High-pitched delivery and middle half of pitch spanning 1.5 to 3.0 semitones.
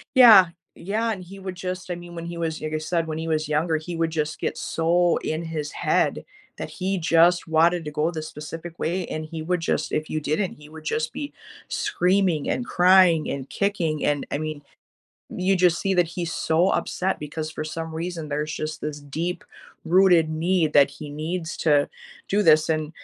No: medium, 165 Hz; narrow, 2.5 semitones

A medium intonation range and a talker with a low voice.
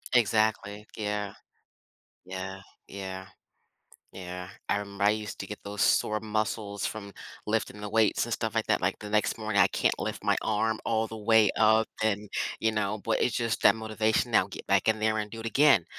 No: narrow, 1.4 semitones; low, 105 Hz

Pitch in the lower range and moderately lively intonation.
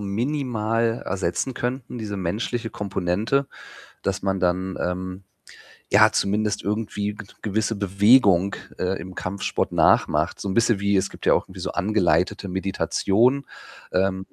Yes: low, 100 Hz; average, 3.0 semitones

